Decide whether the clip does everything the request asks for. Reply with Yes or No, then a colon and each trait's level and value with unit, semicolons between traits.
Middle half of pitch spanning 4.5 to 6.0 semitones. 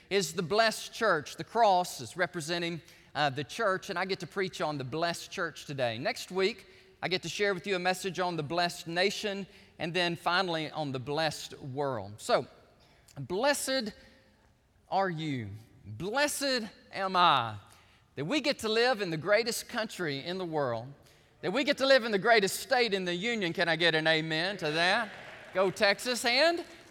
Yes: average, 5.2 semitones